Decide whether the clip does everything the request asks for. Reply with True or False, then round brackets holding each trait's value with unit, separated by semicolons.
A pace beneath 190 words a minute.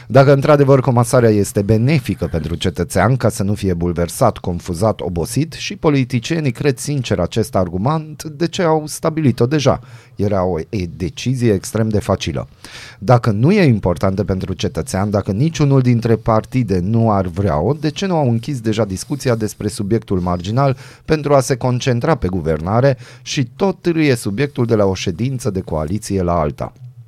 True (165 wpm)